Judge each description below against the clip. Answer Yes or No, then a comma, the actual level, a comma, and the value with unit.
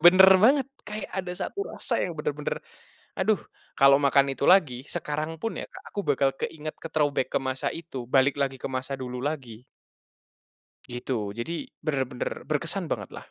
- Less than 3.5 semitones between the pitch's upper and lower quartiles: No, average, 4.8 semitones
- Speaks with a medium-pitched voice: Yes, medium, 145 Hz